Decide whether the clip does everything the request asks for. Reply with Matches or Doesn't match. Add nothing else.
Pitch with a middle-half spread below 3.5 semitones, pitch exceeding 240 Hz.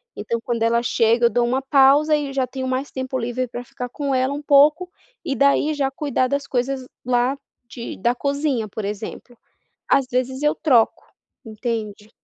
Matches